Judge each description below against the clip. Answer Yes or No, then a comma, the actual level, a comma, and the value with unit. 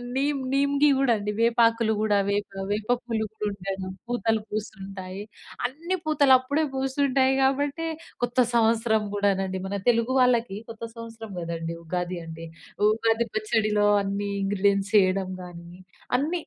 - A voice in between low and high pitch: No, high, 220 Hz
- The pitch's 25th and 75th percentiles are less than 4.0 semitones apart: No, average, 4.4 semitones